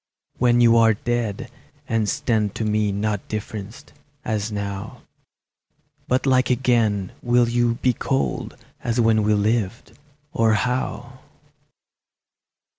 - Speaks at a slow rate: Yes, slow, 115 wpm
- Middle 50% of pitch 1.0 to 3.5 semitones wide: Yes, narrow, 2.4 semitones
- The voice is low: Yes, low, 115 Hz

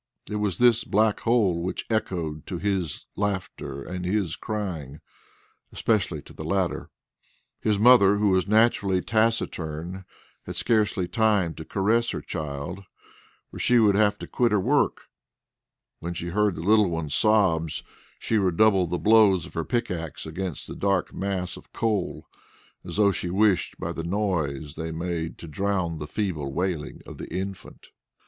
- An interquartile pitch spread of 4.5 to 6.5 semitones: No, average, 4.1 semitones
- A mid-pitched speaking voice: No, very low, 95 Hz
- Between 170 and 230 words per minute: No, average, 160 wpm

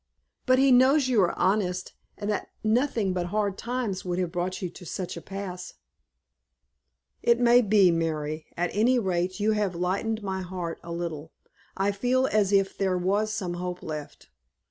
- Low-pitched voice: No, high, 190 Hz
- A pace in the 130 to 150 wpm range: No, average, 180 wpm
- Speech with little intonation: No, average, 3.4 semitones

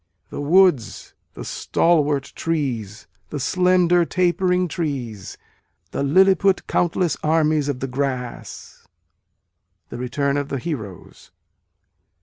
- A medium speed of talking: No, slow, 105 wpm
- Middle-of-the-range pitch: Yes, medium, 150 Hz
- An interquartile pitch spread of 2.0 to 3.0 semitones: No, average, 5.0 semitones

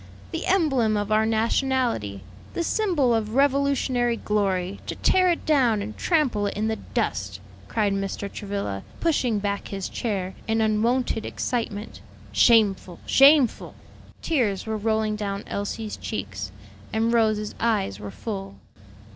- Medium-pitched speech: No, high, 220 Hz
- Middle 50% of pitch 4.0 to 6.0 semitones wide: No, average, 3.6 semitones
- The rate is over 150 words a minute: No, slow, 135 wpm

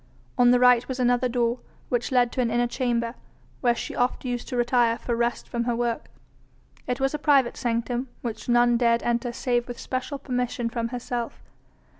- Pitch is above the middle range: Yes, high, 240 Hz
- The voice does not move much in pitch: Yes, narrow, 1.0 semitones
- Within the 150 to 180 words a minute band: No, average, 190 wpm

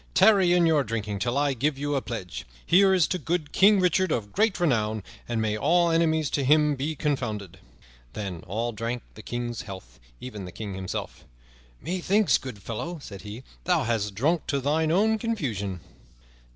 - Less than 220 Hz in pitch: Yes, low, 135 Hz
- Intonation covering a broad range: Yes, wide, 7.8 semitones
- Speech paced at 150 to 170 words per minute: No, average, 180 wpm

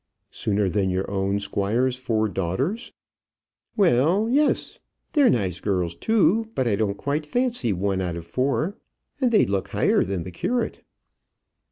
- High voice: No, low, 110 Hz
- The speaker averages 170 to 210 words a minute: No, average, 150 wpm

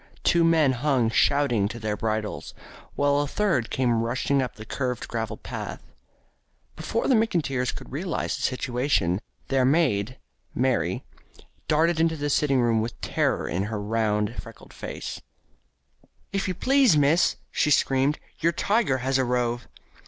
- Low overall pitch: Yes, low, 130 Hz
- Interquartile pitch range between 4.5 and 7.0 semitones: Yes, average, 5.0 semitones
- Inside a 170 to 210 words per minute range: No, average, 145 wpm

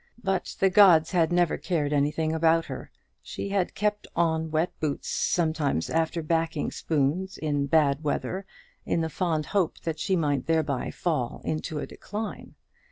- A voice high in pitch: No, medium, 160 Hz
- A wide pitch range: No, average, 2.7 semitones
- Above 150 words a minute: Yes, average, 160 wpm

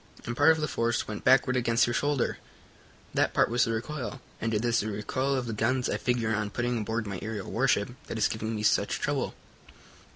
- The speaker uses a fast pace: Yes, fast, 220 wpm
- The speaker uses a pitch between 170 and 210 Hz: No, low, 115 Hz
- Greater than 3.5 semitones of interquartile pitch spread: No, narrow, 2.6 semitones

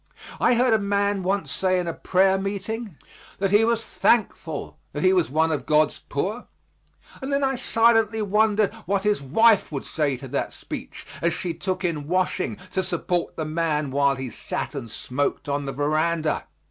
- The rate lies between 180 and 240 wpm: Yes, average, 185 wpm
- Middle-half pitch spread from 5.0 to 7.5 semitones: Yes, wide, 5.4 semitones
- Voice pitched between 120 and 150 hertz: No, medium, 185 Hz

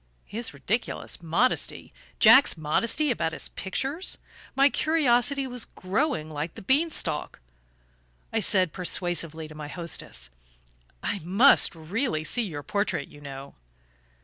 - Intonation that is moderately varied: No, wide, 8.3 semitones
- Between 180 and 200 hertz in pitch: Yes, high, 190 Hz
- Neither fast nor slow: No, slow, 125 wpm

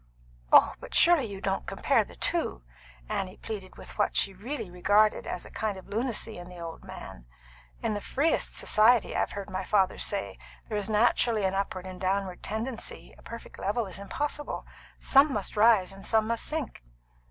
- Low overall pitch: No, high, 205 Hz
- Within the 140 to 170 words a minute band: No, average, 185 wpm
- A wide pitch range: No, average, 3.4 semitones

